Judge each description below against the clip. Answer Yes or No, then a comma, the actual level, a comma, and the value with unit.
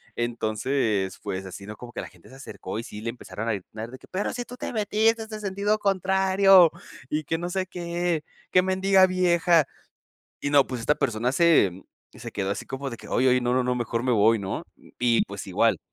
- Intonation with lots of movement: Yes, wide, 8.5 semitones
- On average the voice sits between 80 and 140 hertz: Yes, low, 135 Hz